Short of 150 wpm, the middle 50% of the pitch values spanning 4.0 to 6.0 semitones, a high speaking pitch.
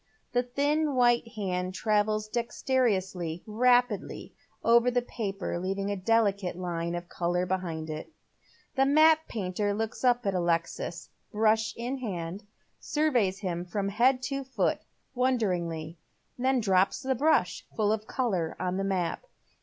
Yes: average, 140 wpm; average, 5.2 semitones; high, 210 Hz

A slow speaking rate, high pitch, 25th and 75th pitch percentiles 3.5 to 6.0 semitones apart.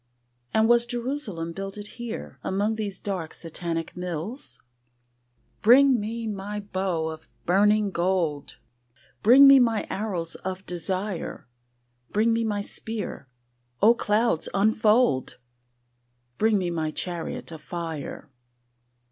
Yes: slow, 115 wpm; high, 200 Hz; average, 4.4 semitones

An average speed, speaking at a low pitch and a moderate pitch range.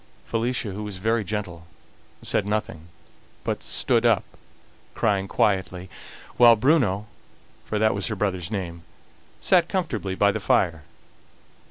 No: slow, 130 wpm; low, 100 Hz; average, 3.2 semitones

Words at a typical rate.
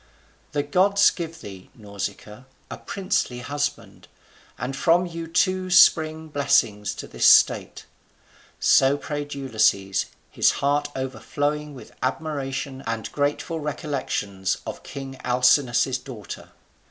No: slow, 115 wpm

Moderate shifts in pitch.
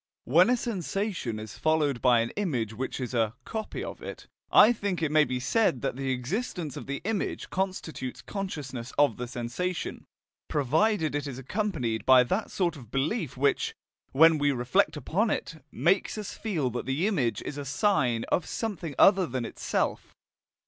No: wide, 7.1 semitones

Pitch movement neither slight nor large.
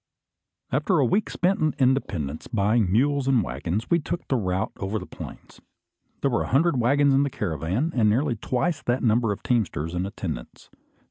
No: wide, 6.1 semitones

